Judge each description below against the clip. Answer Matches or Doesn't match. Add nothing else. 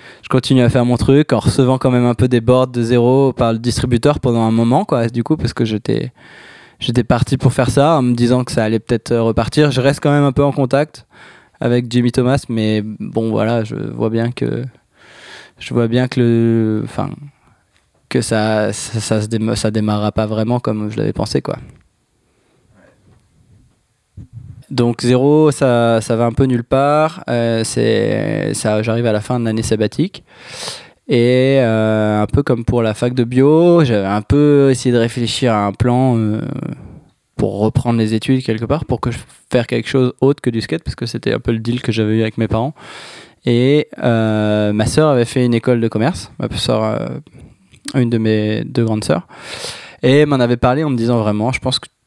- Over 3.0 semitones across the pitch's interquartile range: Doesn't match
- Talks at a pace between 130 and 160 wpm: Doesn't match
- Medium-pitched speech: Doesn't match